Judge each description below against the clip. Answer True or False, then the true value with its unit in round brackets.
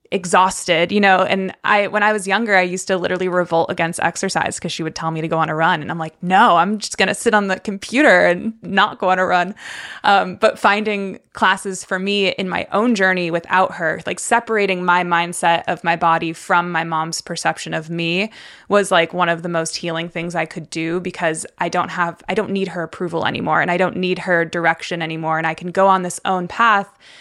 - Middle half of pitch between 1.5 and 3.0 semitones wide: True (2.6 semitones)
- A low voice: False (180 Hz)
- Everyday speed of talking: False (230 wpm)